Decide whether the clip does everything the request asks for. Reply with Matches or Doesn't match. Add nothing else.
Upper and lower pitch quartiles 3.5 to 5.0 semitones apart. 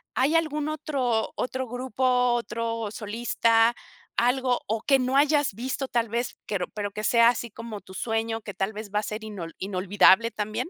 Doesn't match